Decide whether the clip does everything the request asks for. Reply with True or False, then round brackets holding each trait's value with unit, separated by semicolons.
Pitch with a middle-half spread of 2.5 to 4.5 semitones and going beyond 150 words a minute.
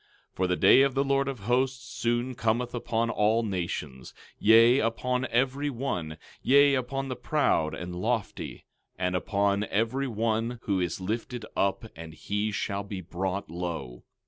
False (5.1 semitones; 160 wpm)